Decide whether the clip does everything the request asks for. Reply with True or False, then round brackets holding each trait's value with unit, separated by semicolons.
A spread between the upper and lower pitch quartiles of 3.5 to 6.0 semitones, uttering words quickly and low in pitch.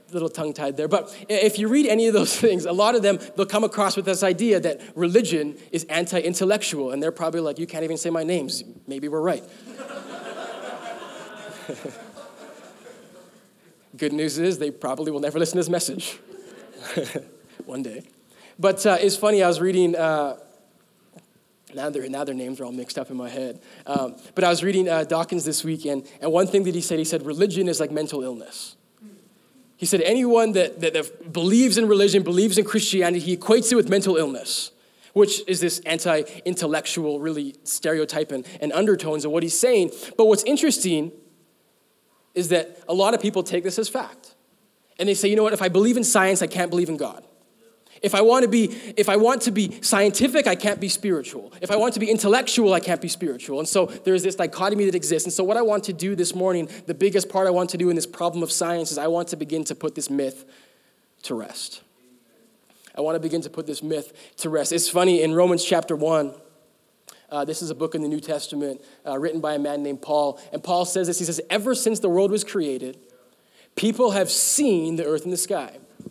False (4.5 semitones; 215 wpm; 175 Hz)